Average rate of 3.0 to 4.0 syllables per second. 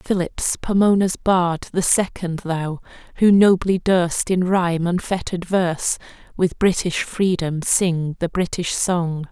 Yes: 3.9 syllables/s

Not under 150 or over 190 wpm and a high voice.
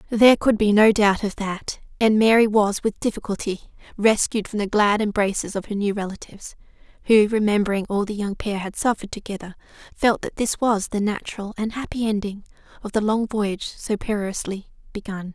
Yes: average, 180 wpm; high, 210 Hz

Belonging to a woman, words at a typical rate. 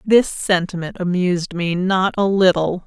Yes: female; average, 145 wpm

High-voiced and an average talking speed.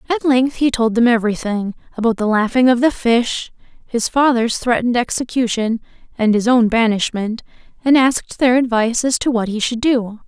Yes: high, 235 Hz; average, 165 wpm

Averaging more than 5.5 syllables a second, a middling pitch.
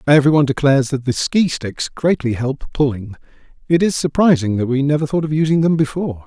Yes: 5.9 syllables/s; medium, 145 Hz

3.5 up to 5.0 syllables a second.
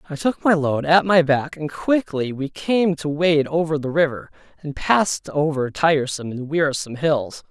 Yes: 4.9 syllables/s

